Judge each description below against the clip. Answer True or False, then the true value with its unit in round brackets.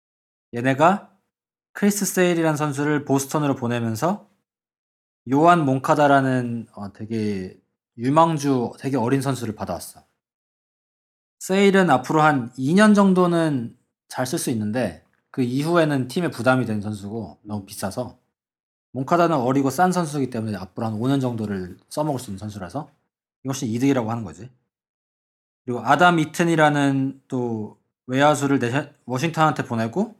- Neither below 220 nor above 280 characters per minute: False (300 characters per minute)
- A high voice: False (135 Hz)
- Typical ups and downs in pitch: True (4.9 semitones)